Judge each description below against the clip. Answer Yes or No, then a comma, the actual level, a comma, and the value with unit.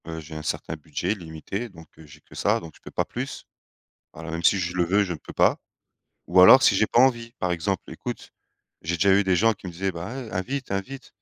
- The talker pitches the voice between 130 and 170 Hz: No, very low, 90 Hz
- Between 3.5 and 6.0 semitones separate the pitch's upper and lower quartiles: Yes, average, 3.8 semitones